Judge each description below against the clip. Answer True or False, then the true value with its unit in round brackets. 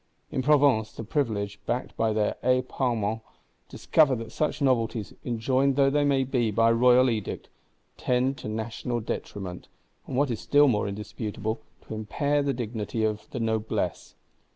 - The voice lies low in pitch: True (115 Hz)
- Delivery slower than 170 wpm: True (155 wpm)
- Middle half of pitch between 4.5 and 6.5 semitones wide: False (3.4 semitones)